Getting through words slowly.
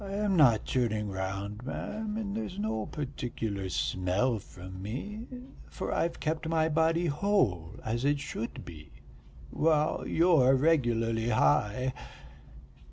Yes: slow, 125 wpm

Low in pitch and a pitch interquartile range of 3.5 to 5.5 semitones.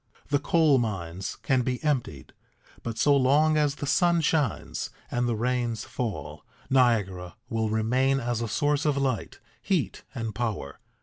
Yes: low, 120 Hz; average, 4.2 semitones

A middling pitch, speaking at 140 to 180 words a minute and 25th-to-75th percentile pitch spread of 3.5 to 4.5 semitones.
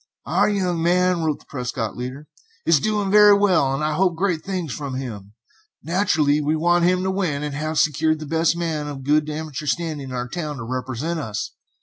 No: medium, 155 Hz; average, 200 wpm; average, 3.8 semitones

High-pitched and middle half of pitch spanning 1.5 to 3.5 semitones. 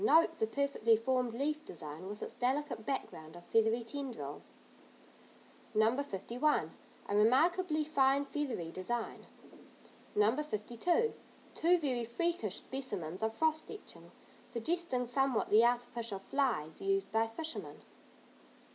No: high, 245 Hz; average, 5.3 semitones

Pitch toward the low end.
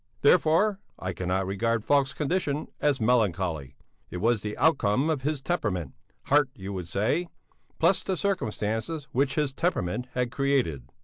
Yes: low, 125 Hz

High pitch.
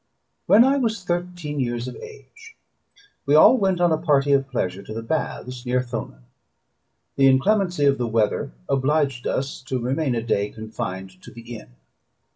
No: low, 135 Hz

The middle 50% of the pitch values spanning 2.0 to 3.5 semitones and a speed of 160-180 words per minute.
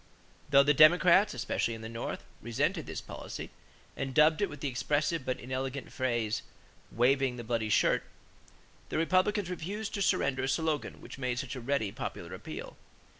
No: average, 4.6 semitones; average, 170 wpm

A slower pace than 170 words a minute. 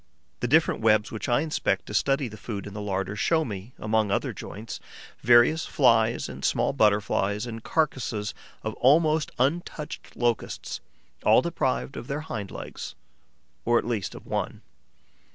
Yes: average, 155 wpm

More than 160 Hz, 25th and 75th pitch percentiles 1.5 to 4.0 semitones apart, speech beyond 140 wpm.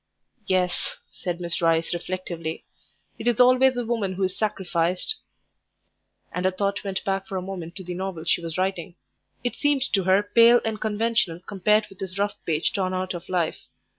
Yes: high, 190 Hz; average, 3.1 semitones; average, 185 wpm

